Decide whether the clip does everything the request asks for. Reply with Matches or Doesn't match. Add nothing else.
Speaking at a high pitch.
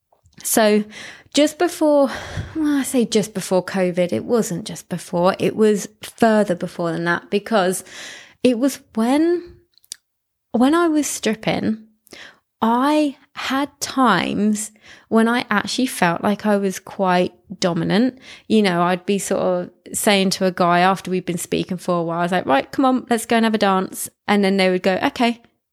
Matches